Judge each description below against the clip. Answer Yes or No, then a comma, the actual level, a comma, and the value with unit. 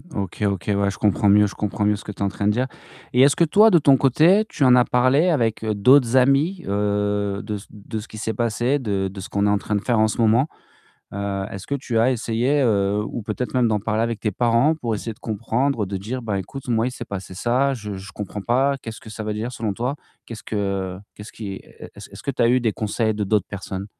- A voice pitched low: Yes, low, 110 Hz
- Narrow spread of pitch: No, average, 3.6 semitones